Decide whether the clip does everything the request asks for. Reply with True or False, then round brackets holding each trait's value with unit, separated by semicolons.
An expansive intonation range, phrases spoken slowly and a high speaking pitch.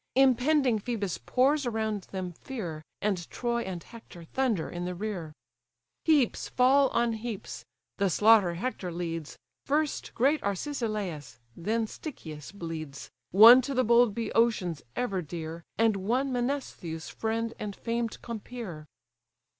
True (5.7 semitones; 130 wpm; 220 Hz)